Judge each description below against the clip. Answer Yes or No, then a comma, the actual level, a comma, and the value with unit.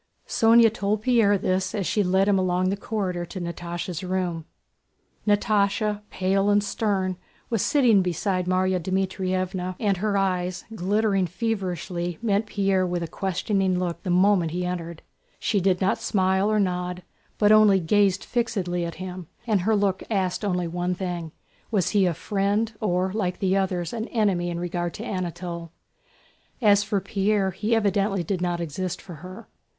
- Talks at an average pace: Yes, average, 165 wpm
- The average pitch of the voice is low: No, high, 190 Hz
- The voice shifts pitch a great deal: No, narrow, 2.4 semitones